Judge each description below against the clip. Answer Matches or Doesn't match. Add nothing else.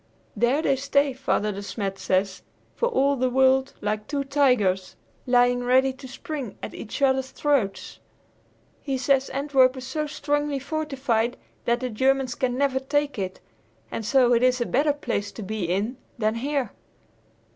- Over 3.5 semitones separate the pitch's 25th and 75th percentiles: Doesn't match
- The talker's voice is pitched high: Matches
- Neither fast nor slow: Matches